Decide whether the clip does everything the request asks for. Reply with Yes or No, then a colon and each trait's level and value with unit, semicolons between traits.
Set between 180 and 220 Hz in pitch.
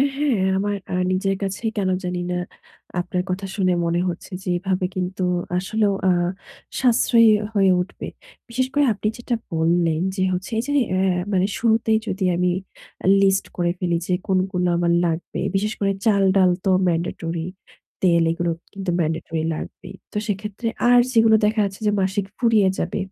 Yes: high, 190 Hz